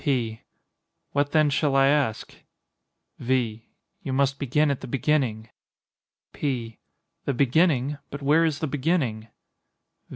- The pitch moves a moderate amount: Yes, average, 3.4 semitones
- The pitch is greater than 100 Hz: Yes, low, 135 Hz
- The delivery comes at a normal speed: No, slow, 125 wpm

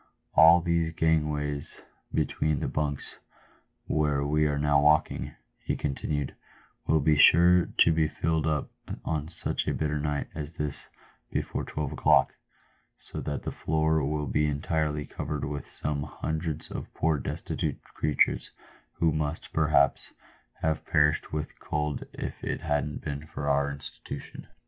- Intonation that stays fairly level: Yes, narrow, 1.4 semitones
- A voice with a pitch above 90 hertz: No, very low, 75 Hz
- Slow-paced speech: No, average, 150 wpm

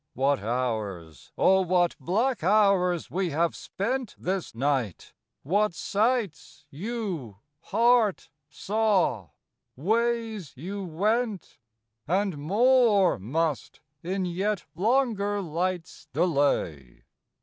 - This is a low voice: No, medium, 185 Hz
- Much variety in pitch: Yes, wide, 6.6 semitones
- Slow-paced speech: Yes, slow, 95 wpm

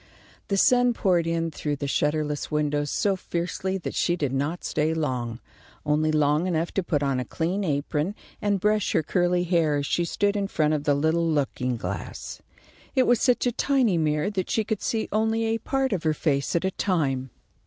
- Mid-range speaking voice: Yes, medium, 165 Hz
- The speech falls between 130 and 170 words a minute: No, average, 200 wpm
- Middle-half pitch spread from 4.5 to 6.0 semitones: Yes, average, 5.0 semitones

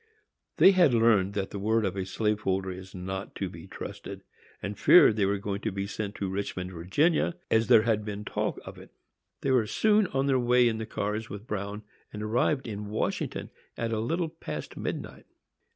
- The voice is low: Yes, low, 105 Hz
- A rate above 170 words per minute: Yes, average, 200 wpm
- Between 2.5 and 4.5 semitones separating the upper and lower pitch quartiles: Yes, average, 3.0 semitones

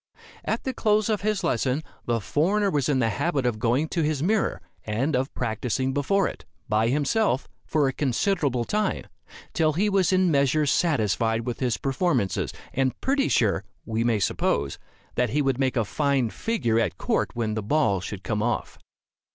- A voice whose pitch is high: No, low, 135 Hz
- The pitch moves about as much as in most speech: No, wide, 6.4 semitones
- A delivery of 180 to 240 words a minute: Yes, average, 185 wpm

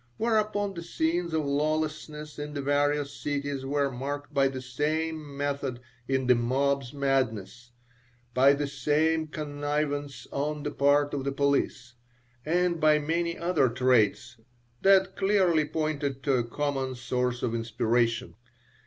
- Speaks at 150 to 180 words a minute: No, slow, 135 wpm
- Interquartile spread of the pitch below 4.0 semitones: Yes, narrow, 2.6 semitones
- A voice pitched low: No, medium, 145 Hz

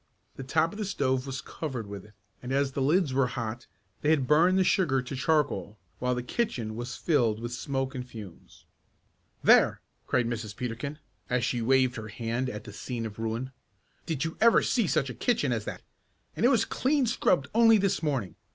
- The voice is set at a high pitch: No, low, 130 Hz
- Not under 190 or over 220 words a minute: Yes, average, 200 wpm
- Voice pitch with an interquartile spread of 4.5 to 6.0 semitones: Yes, average, 5.1 semitones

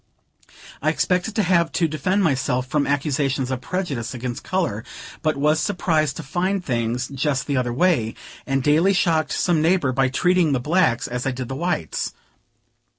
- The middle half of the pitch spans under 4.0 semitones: No, average, 5.3 semitones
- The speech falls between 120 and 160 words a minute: No, average, 170 wpm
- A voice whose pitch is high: No, medium, 150 Hz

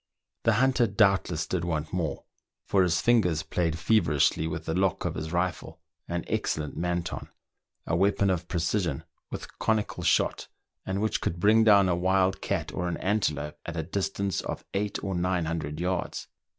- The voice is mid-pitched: No, very low, 90 Hz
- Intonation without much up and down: No, average, 3.3 semitones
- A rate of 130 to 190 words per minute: Yes, average, 170 wpm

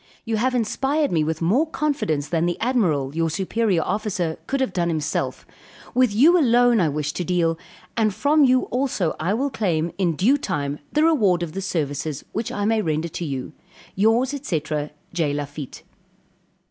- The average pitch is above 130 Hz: Yes, medium, 185 Hz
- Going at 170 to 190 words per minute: Yes, average, 175 wpm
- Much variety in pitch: Yes, wide, 7.5 semitones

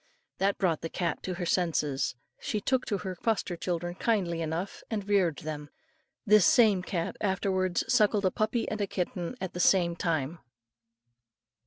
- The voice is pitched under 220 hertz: Yes, medium, 185 Hz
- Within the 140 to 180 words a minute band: Yes, average, 165 wpm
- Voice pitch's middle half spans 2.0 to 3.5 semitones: Yes, average, 3.1 semitones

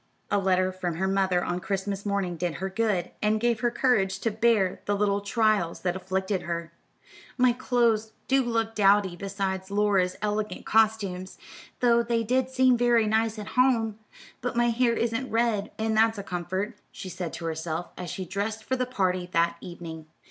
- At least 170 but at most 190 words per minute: Yes, average, 180 wpm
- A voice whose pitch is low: No, high, 205 Hz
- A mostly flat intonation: No, average, 3.5 semitones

